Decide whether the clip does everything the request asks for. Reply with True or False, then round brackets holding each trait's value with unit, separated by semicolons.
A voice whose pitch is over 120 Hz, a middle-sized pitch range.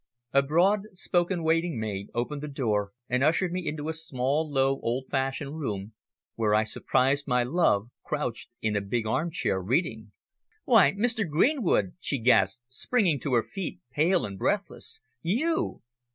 False (140 Hz; 6.5 semitones)